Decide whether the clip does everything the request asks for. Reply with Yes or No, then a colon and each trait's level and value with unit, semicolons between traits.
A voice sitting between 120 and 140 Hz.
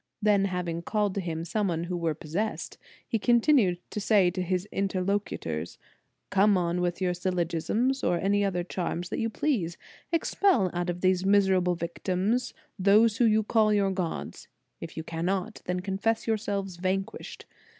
No: high, 190 Hz